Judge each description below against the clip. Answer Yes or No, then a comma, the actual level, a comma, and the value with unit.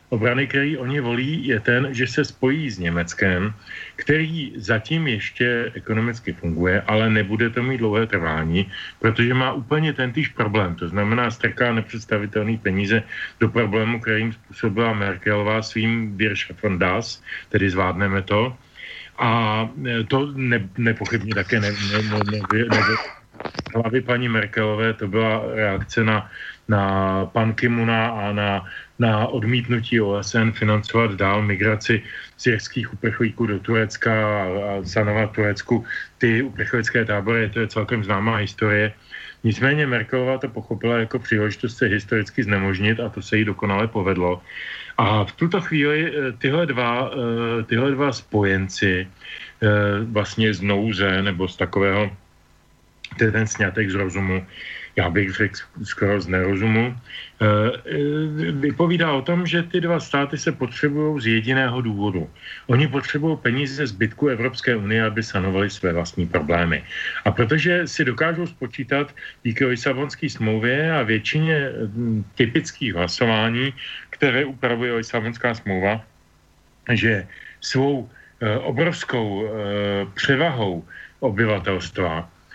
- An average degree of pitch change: Yes, average, 3.7 semitones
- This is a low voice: Yes, low, 110 Hz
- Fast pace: No, average, 130 wpm